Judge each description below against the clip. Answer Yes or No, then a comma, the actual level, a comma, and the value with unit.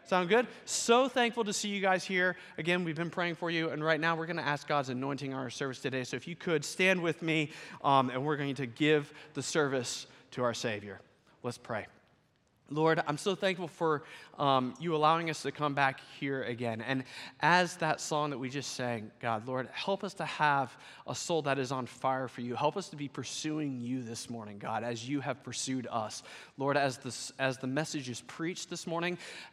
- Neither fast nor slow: No, fast, 215 wpm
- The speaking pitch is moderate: Yes, medium, 145 Hz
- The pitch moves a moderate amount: Yes, average, 4.2 semitones